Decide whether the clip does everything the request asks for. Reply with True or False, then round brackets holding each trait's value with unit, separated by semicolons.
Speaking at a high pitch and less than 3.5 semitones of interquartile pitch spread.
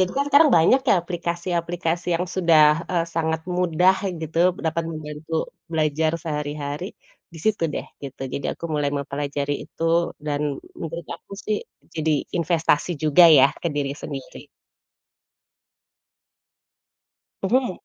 False (165 Hz; 2.8 semitones)